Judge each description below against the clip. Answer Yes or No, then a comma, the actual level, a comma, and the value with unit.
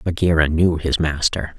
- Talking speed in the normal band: Yes, average, 150 wpm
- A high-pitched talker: No, very low, 80 Hz